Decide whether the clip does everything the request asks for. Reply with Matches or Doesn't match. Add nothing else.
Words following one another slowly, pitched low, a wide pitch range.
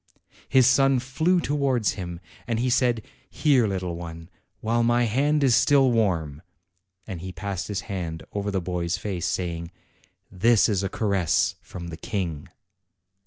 Doesn't match